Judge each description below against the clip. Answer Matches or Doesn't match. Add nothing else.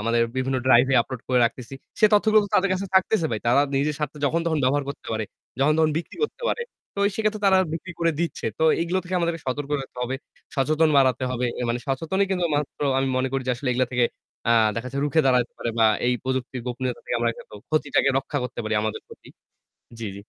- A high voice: Doesn't match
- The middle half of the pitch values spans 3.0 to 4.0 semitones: Doesn't match